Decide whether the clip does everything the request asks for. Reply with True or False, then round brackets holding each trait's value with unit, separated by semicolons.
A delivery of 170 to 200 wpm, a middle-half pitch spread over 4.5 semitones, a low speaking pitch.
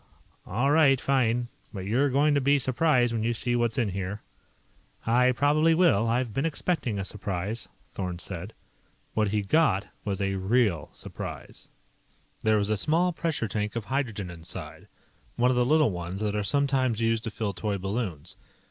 True (175 wpm; 5.2 semitones; 115 Hz)